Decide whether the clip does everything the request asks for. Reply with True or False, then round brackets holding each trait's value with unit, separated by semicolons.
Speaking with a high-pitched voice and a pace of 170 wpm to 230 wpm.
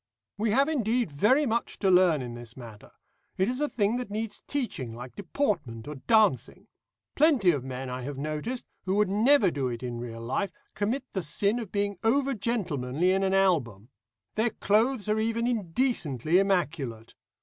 True (195 Hz; 175 wpm)